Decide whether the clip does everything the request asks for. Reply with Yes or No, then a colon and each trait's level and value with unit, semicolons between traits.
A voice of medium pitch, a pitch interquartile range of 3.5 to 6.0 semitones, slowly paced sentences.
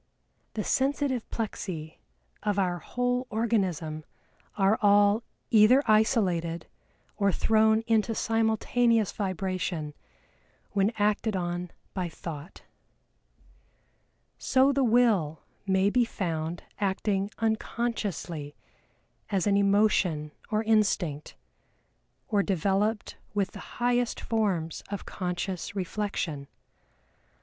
No: high, 200 Hz; average, 3.9 semitones; slow, 95 wpm